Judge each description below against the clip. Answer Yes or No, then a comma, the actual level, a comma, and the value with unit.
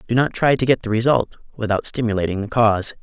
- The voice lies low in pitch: Yes, low, 115 Hz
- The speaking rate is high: Yes, fast, 220 wpm